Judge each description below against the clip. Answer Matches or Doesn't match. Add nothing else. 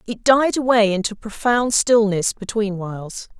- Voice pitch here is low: Doesn't match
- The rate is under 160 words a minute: Matches